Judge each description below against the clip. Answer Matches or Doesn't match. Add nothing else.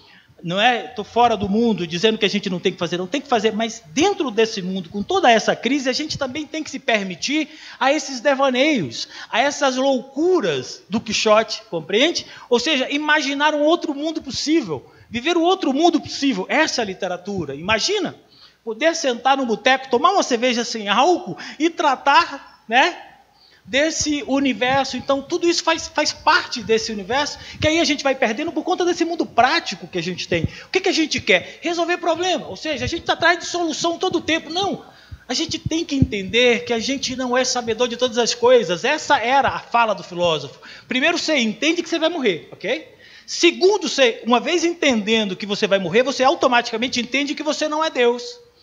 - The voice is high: Matches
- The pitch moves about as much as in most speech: Doesn't match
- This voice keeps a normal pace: Doesn't match